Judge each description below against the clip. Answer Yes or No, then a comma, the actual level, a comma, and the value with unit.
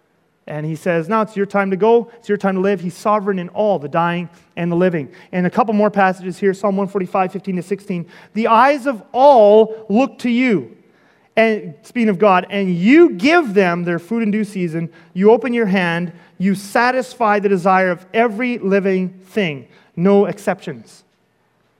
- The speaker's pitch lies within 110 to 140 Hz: No, high, 200 Hz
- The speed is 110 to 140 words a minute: No, average, 185 wpm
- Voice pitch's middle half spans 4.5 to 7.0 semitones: No, average, 3.5 semitones